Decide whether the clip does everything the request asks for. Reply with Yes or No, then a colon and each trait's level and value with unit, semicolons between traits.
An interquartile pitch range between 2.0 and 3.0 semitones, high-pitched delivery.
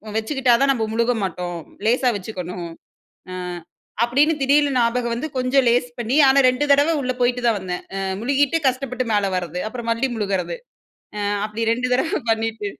No: average, 3.8 semitones; high, 240 Hz